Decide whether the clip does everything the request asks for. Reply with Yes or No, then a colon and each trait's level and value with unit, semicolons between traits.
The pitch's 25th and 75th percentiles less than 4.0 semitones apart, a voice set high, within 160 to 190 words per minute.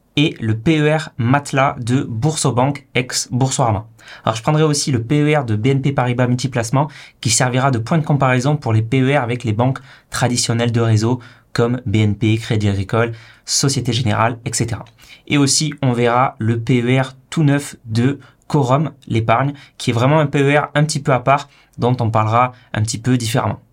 No: average, 3.3 semitones; low, 125 Hz; average, 170 wpm